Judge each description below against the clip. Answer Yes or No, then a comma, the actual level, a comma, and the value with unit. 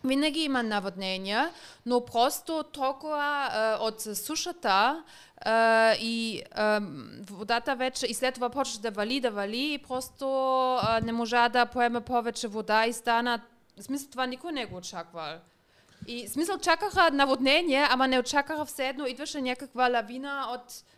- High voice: Yes, very high, 250 Hz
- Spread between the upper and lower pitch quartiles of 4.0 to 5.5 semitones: No, average, 3.6 semitones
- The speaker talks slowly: No, average, 145 wpm